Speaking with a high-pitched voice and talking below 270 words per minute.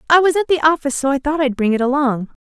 No: very high, 285 Hz; fast, 295 wpm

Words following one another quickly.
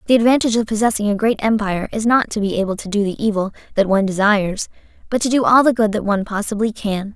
Yes: fast, 245 wpm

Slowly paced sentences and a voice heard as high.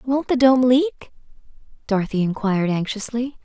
Yes: slow, 120 wpm; high, 230 Hz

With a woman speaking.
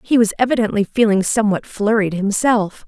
Yes: female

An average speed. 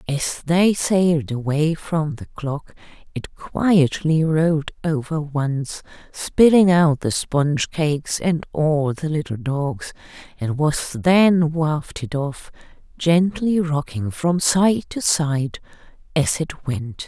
No: slow, 125 wpm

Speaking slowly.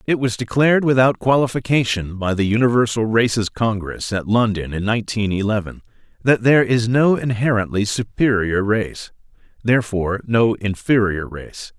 Yes: slow, 130 wpm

